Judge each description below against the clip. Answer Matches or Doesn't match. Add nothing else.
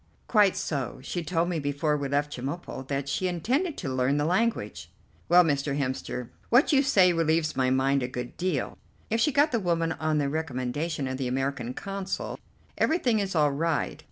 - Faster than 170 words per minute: Matches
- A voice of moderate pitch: Matches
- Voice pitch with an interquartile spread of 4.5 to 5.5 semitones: Matches